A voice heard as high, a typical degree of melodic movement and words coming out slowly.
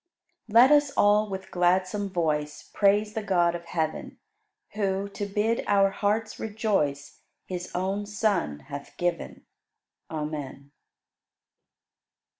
Yes: high, 195 Hz; average, 3.6 semitones; slow, 115 wpm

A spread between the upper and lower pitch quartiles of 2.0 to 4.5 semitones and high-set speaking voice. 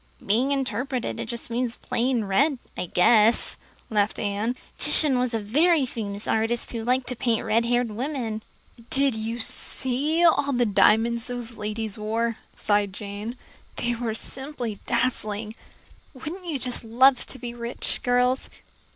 Yes: average, 2.8 semitones; high, 235 Hz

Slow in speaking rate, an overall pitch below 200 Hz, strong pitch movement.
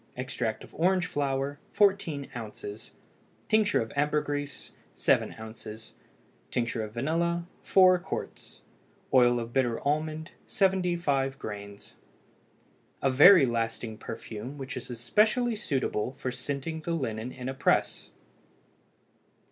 Yes: slow, 115 wpm; low, 135 Hz; wide, 5.8 semitones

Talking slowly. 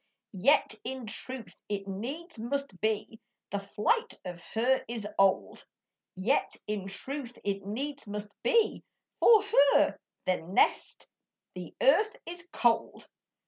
Yes: slow, 120 wpm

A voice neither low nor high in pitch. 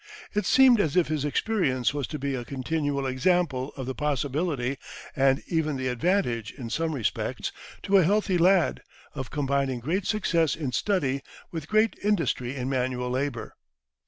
Yes: medium, 145 Hz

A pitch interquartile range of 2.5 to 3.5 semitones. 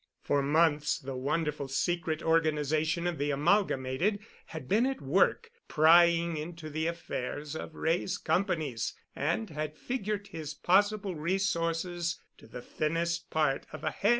Yes: average, 2.8 semitones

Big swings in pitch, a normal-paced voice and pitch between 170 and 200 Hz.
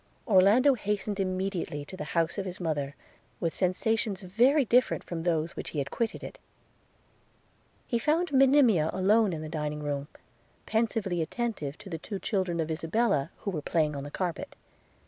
Yes: wide, 5.7 semitones; average, 170 wpm; medium, 185 Hz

